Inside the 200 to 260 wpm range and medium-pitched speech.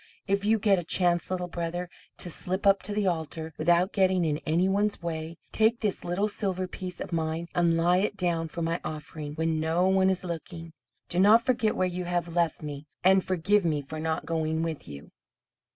Yes: fast, 205 wpm; medium, 175 Hz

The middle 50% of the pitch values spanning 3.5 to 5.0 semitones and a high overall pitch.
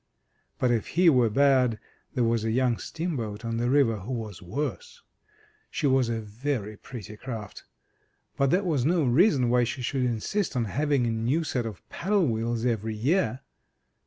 No: average, 4.1 semitones; low, 125 Hz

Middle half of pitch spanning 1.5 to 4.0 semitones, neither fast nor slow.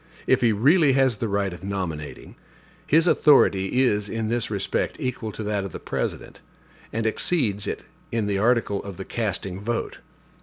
Yes: average, 3.4 semitones; average, 175 wpm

